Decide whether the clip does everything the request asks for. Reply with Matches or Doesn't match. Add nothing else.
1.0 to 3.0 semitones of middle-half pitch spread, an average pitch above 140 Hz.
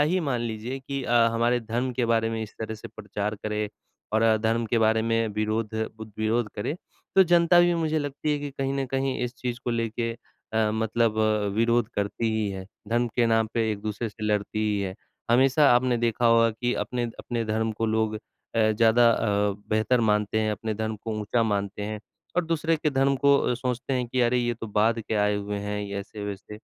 Doesn't match